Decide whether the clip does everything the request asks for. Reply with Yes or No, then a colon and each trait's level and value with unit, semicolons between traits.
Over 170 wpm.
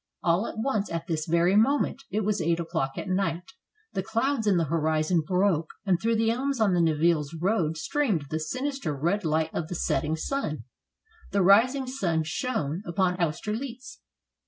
Yes: average, 180 wpm